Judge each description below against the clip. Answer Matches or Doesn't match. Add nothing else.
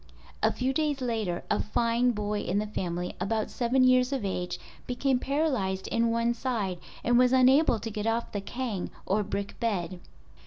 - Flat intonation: Doesn't match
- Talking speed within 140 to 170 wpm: Doesn't match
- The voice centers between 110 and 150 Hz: Doesn't match